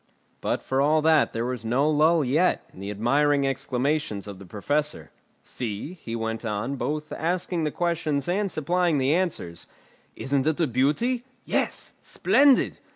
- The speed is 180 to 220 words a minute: No, average, 155 wpm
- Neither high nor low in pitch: Yes, medium, 145 Hz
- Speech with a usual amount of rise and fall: Yes, average, 4.9 semitones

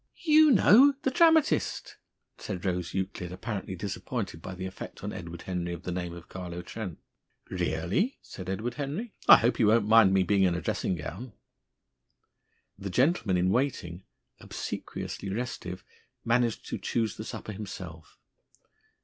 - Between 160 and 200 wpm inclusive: No, average, 150 wpm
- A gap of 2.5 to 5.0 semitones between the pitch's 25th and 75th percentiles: No, wide, 5.4 semitones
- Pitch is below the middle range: Yes, very low, 95 Hz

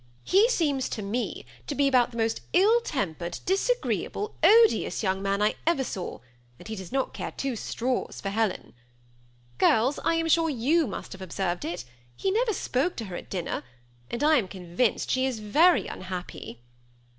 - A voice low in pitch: No, high, 245 Hz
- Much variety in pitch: Yes, wide, 8.8 semitones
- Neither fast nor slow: Yes, average, 180 wpm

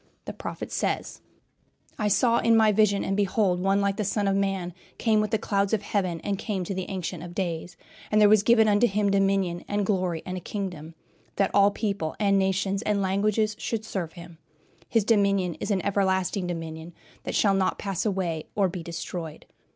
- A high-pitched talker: Yes, high, 195 Hz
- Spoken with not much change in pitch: Yes, narrow, 2.3 semitones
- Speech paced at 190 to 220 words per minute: Yes, average, 195 wpm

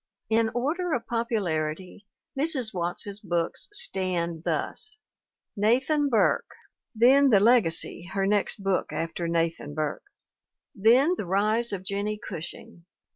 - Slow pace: Yes, slow, 120 wpm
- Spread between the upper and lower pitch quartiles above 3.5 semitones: Yes, wide, 5.5 semitones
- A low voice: No, high, 205 Hz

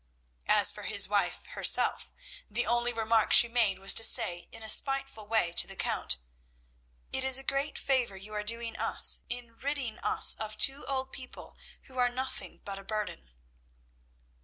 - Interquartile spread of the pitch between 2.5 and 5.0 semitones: Yes, average, 3.6 semitones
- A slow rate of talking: No, average, 175 wpm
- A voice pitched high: Yes, high, 230 Hz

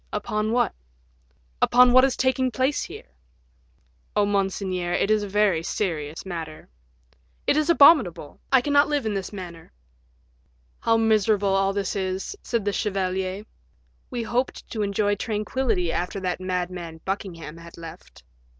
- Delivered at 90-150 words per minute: Yes, average, 140 wpm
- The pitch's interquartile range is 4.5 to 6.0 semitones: No, average, 3.9 semitones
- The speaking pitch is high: Yes, high, 200 Hz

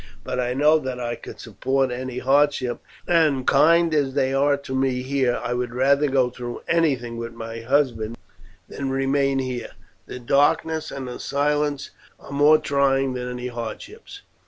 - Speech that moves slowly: No, average, 165 wpm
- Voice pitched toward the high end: No, low, 135 Hz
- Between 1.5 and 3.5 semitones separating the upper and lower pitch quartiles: Yes, narrow, 2.5 semitones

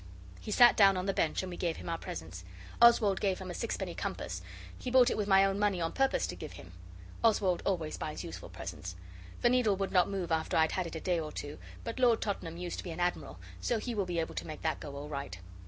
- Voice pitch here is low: No, medium, 185 Hz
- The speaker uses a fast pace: Yes, fast, 255 wpm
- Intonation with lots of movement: No, average, 4.2 semitones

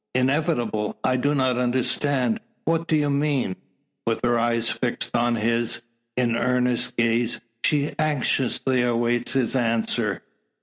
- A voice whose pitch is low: Yes, low, 125 Hz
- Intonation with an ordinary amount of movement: Yes, average, 3.0 semitones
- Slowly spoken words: Yes, slow, 130 wpm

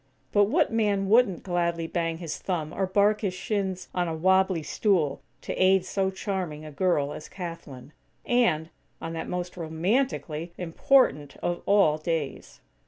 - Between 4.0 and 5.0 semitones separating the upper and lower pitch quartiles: No, average, 3.3 semitones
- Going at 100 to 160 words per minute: Yes, average, 155 wpm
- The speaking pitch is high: No, medium, 180 Hz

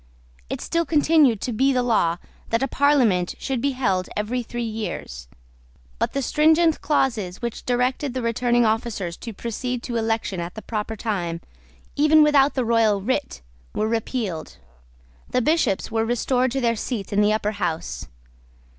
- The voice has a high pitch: Yes, high, 235 Hz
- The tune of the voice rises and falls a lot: No, average, 3.9 semitones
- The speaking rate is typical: Yes, average, 165 wpm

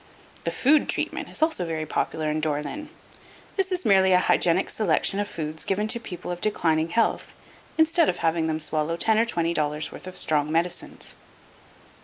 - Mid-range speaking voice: Yes, medium, 175 Hz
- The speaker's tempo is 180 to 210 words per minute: Yes, average, 185 wpm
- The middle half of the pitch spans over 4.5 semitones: Yes, wide, 5.4 semitones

